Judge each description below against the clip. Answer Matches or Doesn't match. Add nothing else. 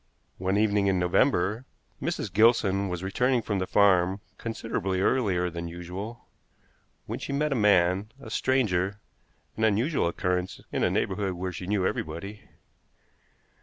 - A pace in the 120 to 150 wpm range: Matches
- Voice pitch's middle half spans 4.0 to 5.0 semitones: Doesn't match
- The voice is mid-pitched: Doesn't match